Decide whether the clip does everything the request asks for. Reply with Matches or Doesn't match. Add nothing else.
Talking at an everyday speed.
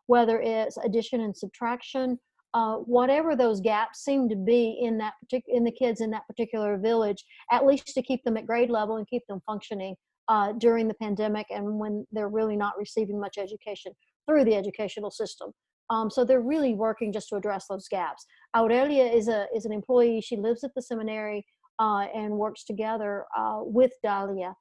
Matches